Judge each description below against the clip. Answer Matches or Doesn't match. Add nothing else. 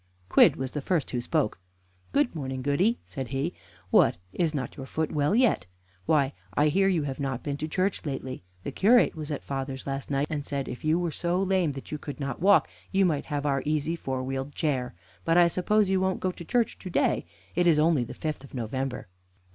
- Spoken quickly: Matches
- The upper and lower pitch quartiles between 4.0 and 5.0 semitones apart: Matches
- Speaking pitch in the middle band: Matches